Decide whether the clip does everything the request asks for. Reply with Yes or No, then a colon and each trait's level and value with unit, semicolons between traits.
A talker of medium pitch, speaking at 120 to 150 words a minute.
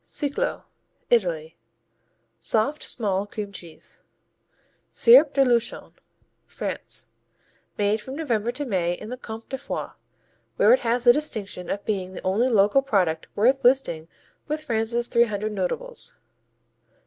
No: high, 225 Hz; slow, 135 wpm